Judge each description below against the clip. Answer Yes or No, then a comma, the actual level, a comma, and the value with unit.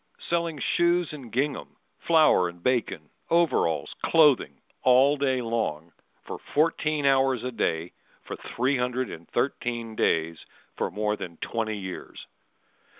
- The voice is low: Yes, low, 125 Hz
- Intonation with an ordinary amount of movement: No, wide, 5.9 semitones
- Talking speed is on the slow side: Yes, slow, 130 wpm